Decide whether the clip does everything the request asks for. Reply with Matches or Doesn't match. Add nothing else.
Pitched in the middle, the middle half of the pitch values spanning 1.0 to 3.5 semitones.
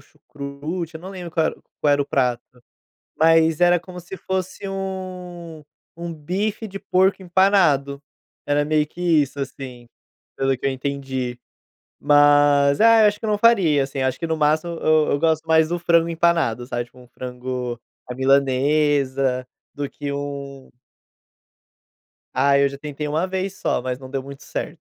Doesn't match